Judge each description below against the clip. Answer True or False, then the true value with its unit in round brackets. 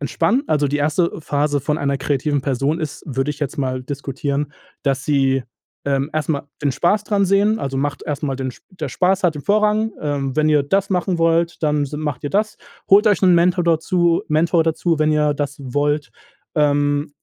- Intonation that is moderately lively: True (3.3 semitones)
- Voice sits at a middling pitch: True (150 Hz)